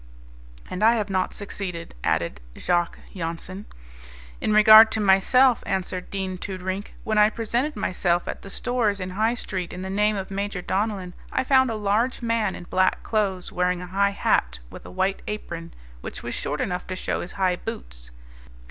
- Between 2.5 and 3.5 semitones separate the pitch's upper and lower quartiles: Yes, average, 2.8 semitones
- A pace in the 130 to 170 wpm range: No, average, 180 wpm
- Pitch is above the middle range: Yes, high, 195 Hz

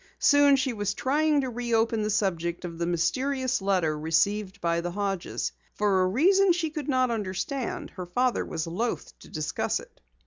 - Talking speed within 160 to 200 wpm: Yes, average, 175 wpm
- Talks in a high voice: Yes, high, 210 Hz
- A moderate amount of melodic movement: No, wide, 6.7 semitones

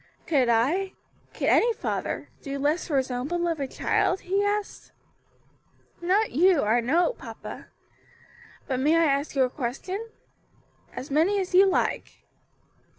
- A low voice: No, very high, 320 Hz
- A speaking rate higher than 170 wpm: No, average, 145 wpm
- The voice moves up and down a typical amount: No, wide, 5.8 semitones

